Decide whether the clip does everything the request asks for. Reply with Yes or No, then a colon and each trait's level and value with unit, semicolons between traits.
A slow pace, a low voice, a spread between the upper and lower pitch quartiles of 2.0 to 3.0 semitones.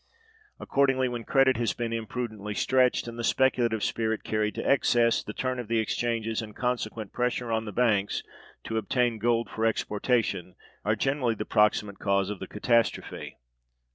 No: average, 165 wpm; low, 115 Hz; narrow, 2.4 semitones